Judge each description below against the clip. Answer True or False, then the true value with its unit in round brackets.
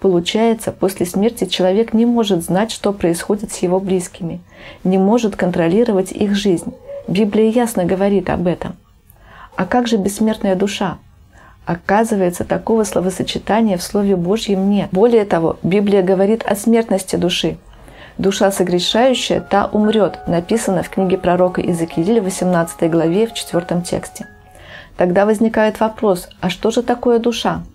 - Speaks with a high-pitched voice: True (195 Hz)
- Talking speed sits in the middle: True (135 wpm)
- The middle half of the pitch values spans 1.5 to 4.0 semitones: True (3.4 semitones)